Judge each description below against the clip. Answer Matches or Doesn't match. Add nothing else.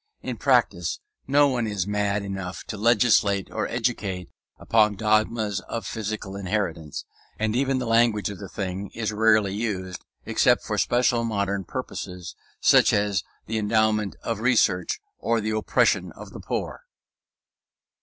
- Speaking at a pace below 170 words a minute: Matches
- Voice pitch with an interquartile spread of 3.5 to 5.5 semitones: Doesn't match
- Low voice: Matches